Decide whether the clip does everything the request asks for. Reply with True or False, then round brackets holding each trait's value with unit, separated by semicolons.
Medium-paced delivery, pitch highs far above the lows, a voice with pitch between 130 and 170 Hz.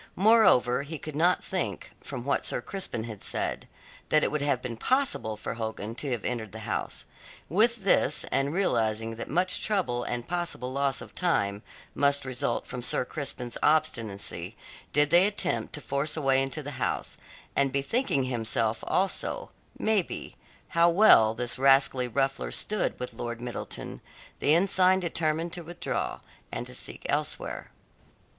True (160 wpm; 6.1 semitones; 140 Hz)